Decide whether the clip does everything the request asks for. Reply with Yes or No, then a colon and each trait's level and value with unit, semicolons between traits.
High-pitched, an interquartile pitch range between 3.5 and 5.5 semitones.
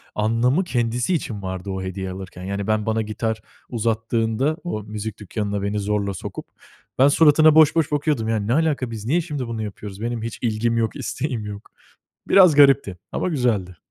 No: low, 115 Hz; average, 4.9 semitones